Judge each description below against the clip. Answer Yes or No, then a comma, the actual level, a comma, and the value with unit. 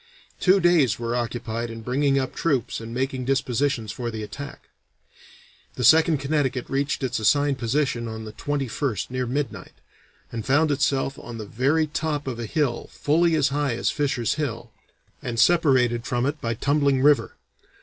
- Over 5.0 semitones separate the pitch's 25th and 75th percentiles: No, average, 3.7 semitones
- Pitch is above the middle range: No, low, 135 Hz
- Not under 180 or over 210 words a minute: No, average, 165 wpm